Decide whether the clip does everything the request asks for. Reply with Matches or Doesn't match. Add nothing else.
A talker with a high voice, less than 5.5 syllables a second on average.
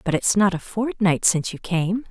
Matches